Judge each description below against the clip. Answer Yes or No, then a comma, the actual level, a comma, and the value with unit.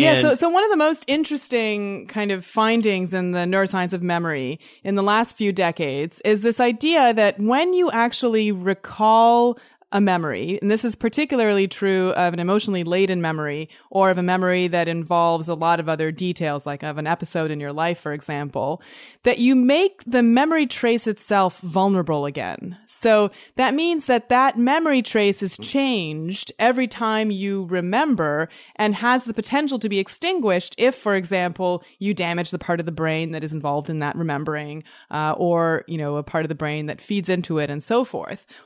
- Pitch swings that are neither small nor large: No, wide, 5.8 semitones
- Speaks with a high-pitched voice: Yes, high, 195 Hz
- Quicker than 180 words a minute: Yes, average, 190 wpm